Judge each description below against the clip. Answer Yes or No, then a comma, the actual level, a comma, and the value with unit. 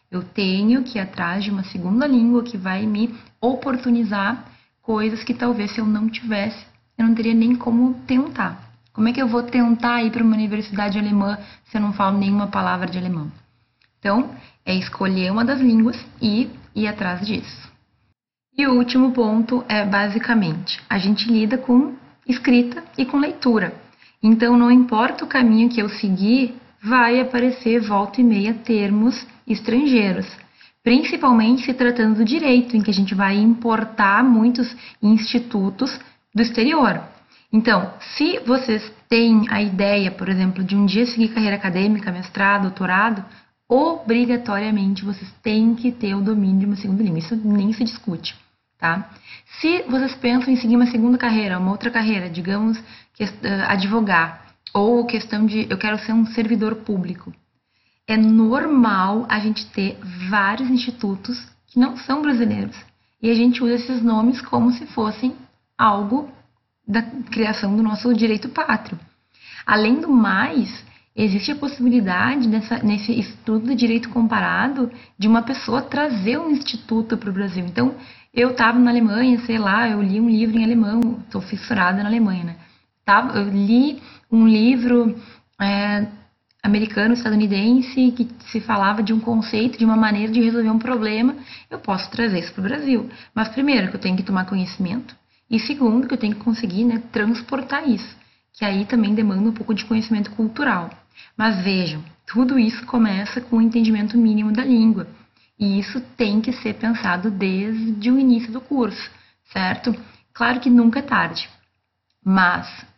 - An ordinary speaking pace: Yes, average, 160 wpm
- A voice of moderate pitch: No, high, 225 Hz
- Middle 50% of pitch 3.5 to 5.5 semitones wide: No, average, 3.1 semitones